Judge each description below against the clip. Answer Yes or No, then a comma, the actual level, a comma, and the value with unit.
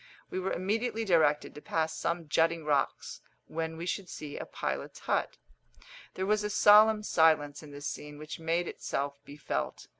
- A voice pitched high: No, medium, 165 Hz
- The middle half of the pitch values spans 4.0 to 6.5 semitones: Yes, average, 4.3 semitones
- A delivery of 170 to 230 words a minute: Yes, average, 175 wpm